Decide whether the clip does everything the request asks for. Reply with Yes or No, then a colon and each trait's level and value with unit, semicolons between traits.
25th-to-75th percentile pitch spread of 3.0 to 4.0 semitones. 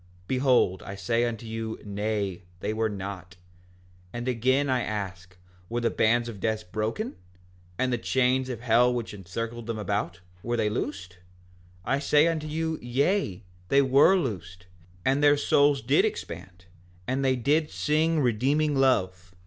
No: average, 4.8 semitones